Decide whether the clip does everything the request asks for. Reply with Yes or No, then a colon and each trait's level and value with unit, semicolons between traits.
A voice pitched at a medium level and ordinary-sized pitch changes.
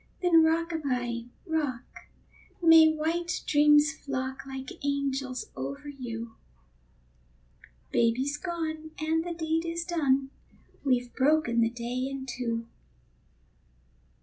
No: very high, 280 Hz; average, 4.1 semitones